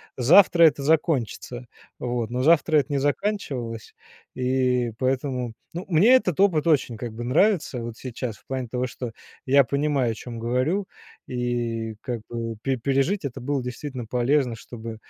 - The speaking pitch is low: Yes, low, 130 Hz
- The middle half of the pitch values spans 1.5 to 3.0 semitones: No, average, 3.6 semitones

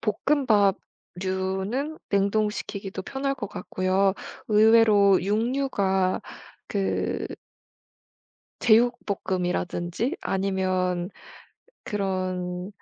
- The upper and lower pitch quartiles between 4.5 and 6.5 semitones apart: No, average, 2.8 semitones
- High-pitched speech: Yes, high, 200 Hz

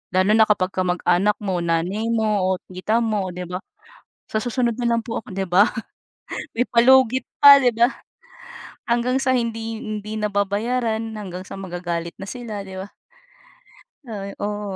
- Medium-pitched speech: No, high, 210 Hz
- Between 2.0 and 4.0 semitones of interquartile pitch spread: Yes, average, 3.6 semitones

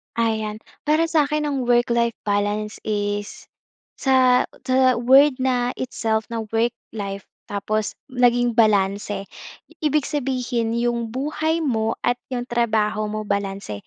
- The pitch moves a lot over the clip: No, average, 3.3 semitones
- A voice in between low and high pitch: No, high, 235 Hz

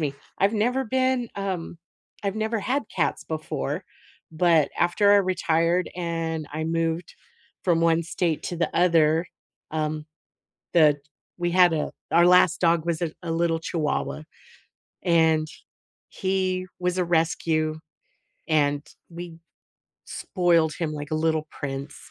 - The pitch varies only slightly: Yes, narrow, 2.3 semitones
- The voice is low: No, medium, 170 Hz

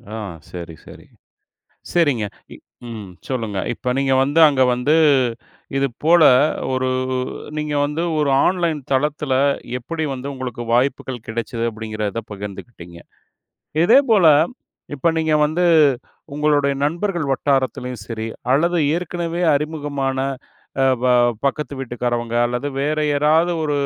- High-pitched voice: No, medium, 140 Hz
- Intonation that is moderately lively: Yes, average, 4.2 semitones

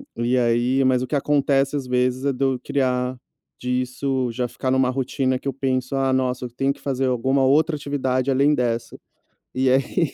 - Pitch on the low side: Yes, low, 130 Hz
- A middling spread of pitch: No, narrow, 1.4 semitones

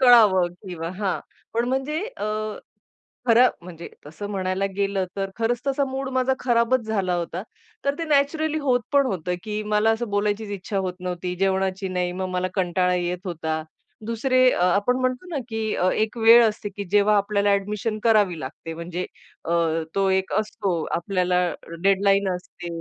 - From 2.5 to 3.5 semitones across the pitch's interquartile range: No, average, 4.0 semitones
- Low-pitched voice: No, high, 200 Hz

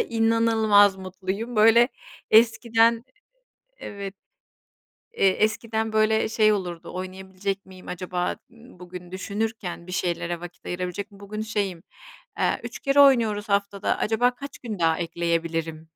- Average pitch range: Yes, average, 3.6 semitones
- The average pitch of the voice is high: Yes, high, 200 Hz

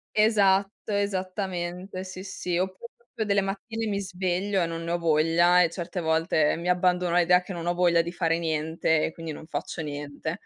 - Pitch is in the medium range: Yes, medium, 180 Hz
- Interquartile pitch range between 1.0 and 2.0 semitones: No, narrow, 2.4 semitones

